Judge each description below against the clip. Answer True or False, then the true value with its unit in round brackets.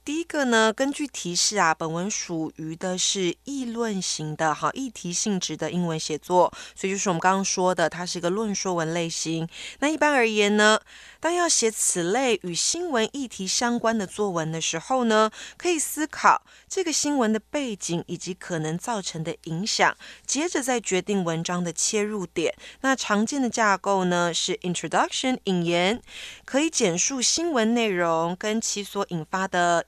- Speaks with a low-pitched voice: False (195 Hz)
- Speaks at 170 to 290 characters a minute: True (280 characters per minute)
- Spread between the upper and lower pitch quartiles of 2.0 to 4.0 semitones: False (5.5 semitones)